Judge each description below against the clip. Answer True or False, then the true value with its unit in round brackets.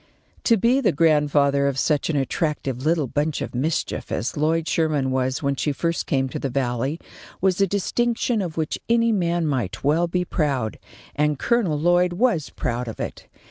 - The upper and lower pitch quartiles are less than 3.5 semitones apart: False (4.1 semitones)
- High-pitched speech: False (155 Hz)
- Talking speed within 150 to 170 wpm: False (180 wpm)